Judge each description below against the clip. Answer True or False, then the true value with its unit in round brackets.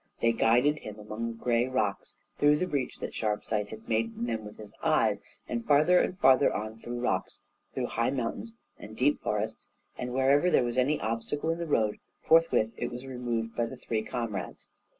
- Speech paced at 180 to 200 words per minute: True (195 wpm)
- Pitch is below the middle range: True (120 Hz)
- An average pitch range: True (3.6 semitones)